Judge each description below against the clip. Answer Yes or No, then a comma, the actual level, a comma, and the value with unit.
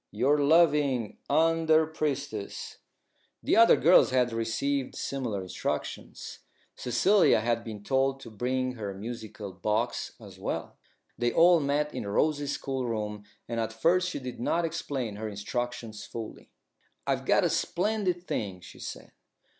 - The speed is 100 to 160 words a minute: Yes, average, 140 wpm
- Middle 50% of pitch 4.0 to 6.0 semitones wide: Yes, wide, 5.4 semitones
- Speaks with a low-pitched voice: Yes, low, 125 Hz